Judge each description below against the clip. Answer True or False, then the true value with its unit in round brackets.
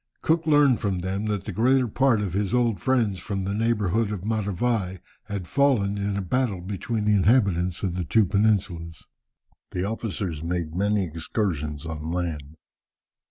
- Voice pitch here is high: False (100 Hz)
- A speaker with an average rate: True (160 wpm)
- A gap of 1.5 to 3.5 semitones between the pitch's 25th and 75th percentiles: False (3.9 semitones)